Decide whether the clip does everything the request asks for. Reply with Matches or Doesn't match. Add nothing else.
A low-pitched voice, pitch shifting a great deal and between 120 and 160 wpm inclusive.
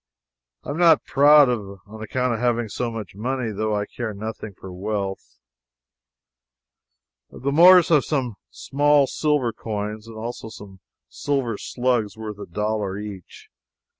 Doesn't match